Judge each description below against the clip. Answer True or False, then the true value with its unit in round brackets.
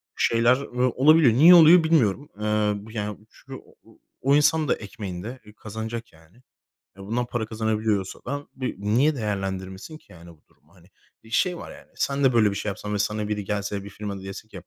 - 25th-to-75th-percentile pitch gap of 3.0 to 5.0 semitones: True (4.3 semitones)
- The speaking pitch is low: True (110 Hz)